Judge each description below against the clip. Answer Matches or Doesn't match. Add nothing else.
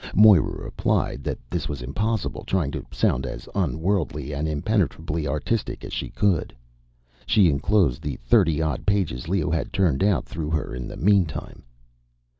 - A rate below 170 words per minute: Matches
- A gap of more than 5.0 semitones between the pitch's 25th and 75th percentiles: Matches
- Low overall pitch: Matches